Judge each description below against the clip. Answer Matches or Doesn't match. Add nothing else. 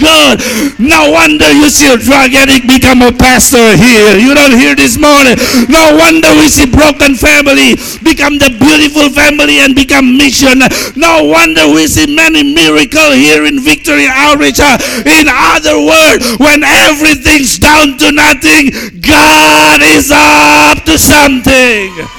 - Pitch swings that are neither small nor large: Matches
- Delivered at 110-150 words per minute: Matches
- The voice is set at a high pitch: Matches